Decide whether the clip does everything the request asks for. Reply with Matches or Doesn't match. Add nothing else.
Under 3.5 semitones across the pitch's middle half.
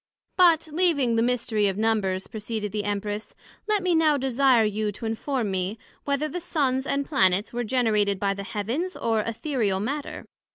Doesn't match